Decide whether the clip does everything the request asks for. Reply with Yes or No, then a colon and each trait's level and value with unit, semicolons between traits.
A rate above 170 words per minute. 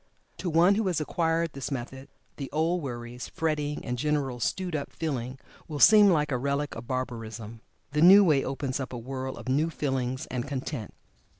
Yes: average, 185 wpm